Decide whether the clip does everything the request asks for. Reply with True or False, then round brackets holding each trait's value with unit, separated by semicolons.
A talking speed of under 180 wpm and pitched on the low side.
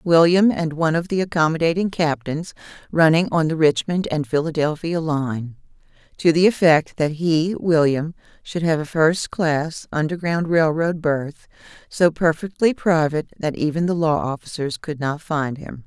False (155 wpm; 160 Hz)